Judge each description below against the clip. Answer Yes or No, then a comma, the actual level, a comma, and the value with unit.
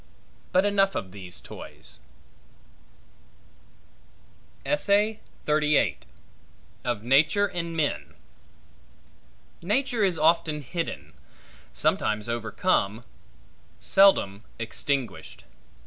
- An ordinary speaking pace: No, slow, 65 wpm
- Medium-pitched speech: Yes, medium, 150 Hz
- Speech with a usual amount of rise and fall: No, wide, 9.0 semitones